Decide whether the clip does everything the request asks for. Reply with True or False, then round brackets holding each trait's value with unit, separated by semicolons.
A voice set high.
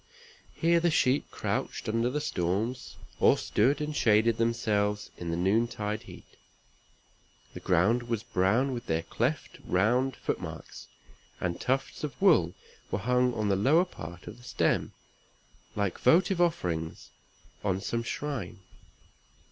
False (115 Hz)